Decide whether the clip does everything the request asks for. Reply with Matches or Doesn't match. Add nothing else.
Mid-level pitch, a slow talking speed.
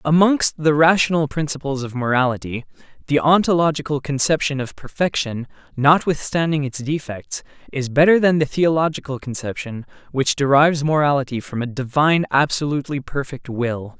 Matches